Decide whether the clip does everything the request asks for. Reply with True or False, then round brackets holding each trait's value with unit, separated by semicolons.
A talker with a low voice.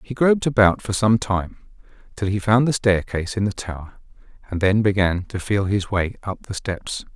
True (100 Hz)